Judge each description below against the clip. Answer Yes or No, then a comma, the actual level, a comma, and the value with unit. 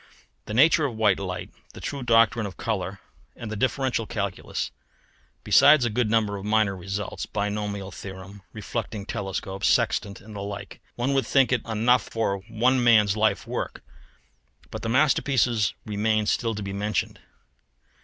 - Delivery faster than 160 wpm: No, average, 155 wpm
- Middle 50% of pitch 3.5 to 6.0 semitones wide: No, average, 2.8 semitones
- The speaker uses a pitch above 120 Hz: No, low, 110 Hz